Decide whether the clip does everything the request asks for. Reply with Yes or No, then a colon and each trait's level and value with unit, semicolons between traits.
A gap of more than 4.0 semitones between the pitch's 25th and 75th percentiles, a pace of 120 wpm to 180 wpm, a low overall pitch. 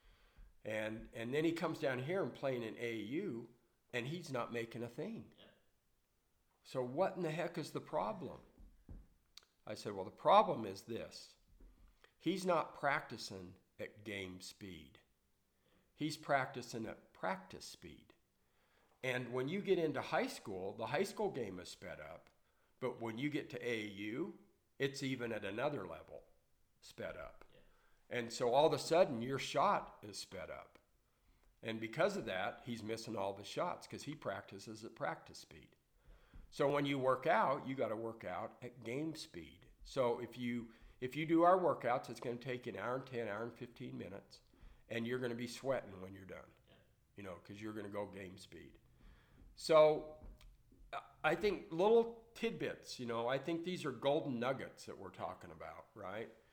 Yes: average, 5.1 semitones; average, 170 wpm; low, 125 Hz